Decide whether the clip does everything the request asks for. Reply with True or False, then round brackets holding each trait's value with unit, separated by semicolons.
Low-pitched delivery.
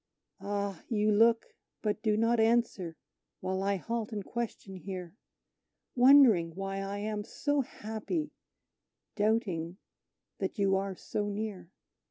False (205 Hz)